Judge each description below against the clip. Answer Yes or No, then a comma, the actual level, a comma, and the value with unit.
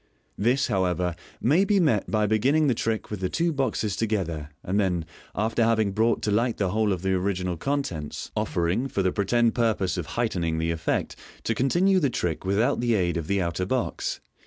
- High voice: No, low, 105 Hz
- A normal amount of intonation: Yes, average, 4.8 semitones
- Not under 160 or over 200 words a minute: Yes, average, 195 wpm